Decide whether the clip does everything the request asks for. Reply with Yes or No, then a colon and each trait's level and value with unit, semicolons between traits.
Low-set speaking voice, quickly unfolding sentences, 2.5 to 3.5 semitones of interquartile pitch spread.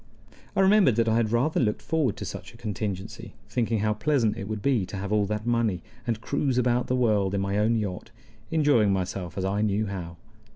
Yes: low, 110 Hz; fast, 215 wpm; average, 3.2 semitones